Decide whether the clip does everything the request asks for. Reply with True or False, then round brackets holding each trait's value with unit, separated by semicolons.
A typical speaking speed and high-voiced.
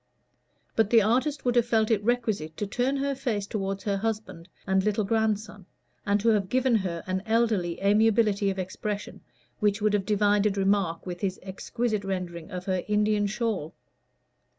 True (170 wpm; 205 Hz)